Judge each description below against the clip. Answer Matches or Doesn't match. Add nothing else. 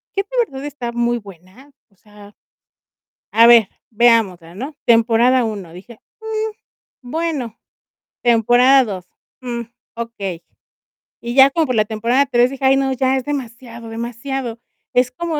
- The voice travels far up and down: Doesn't match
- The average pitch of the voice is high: Matches